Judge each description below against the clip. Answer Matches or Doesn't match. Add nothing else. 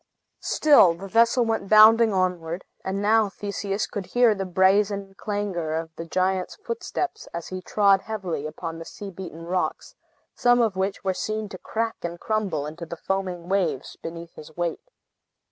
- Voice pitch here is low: Doesn't match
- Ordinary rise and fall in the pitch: Matches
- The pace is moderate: Matches